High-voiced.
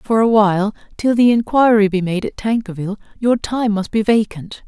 Yes: high, 215 Hz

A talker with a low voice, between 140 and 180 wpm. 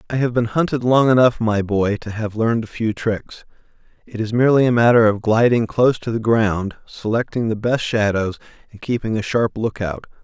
No: low, 115 Hz; average, 200 wpm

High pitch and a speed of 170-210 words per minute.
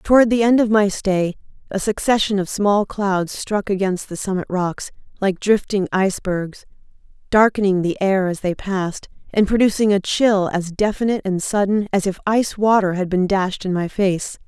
Yes: high, 195 Hz; average, 180 wpm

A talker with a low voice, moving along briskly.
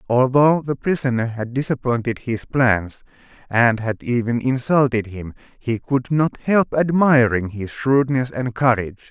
No: low, 125 Hz; average, 140 wpm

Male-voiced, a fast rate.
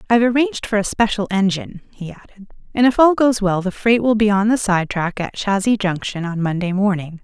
No: female; fast, 215 wpm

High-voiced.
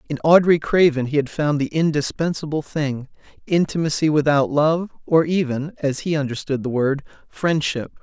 No: medium, 150 Hz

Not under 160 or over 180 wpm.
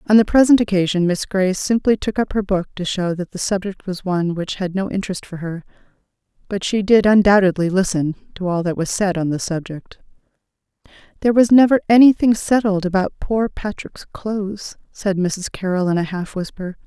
No: average, 190 wpm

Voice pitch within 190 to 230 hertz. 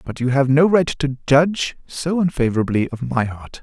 No: medium, 140 Hz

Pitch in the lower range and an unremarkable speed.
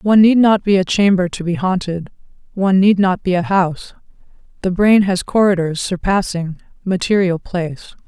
No: high, 190 Hz; average, 165 wpm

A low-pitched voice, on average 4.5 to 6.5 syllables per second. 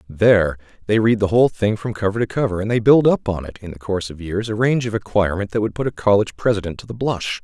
No: low, 105 Hz; 6.8 syllables/s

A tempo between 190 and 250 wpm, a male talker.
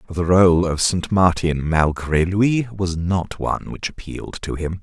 No: average, 175 wpm; male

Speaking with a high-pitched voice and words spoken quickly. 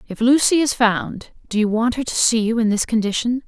Yes: high, 230 Hz; fast, 240 wpm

